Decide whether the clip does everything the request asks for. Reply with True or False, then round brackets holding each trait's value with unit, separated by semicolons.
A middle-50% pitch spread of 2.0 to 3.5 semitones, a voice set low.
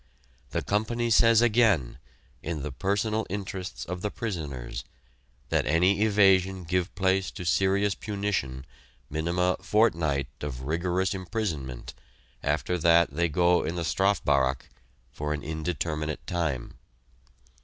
False (4.5 semitones; 90 Hz)